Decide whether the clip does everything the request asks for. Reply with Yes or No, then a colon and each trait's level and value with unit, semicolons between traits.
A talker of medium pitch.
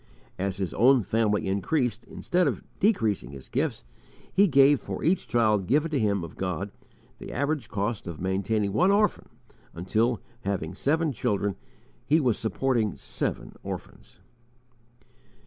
No: low, 110 Hz